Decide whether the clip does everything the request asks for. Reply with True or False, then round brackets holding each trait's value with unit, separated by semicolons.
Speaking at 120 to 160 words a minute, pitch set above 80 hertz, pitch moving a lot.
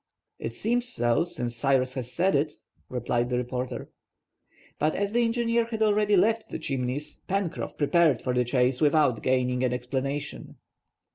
True (155 wpm; 140 Hz; 7.9 semitones)